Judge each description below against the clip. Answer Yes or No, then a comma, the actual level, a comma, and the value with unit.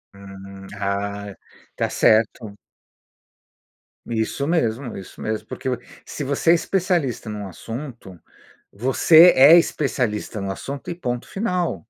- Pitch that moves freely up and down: Yes, wide, 6.7 semitones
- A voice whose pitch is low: Yes, low, 120 Hz